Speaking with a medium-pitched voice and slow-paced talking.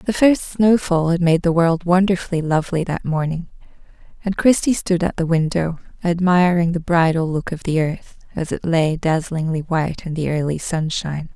No: medium, 170 Hz; average, 180 wpm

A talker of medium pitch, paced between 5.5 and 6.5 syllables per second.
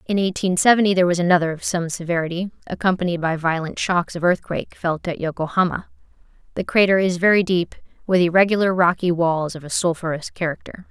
Yes: medium, 175 Hz; 6.1 syllables/s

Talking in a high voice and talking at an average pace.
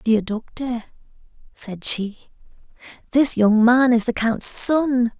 No: high, 235 Hz; slow, 125 wpm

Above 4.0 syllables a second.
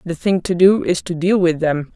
Yes: 4.9 syllables/s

